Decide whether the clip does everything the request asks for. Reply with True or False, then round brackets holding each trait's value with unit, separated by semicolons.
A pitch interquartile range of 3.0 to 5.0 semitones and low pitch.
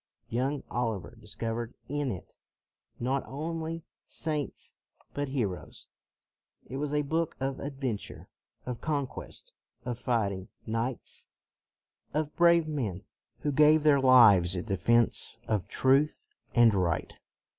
True (4.7 semitones; 130 Hz)